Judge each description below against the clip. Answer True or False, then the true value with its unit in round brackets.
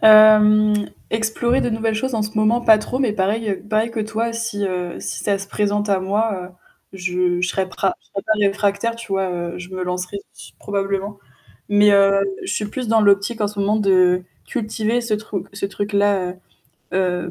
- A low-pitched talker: False (205 Hz)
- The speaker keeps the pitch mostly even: True (2.1 semitones)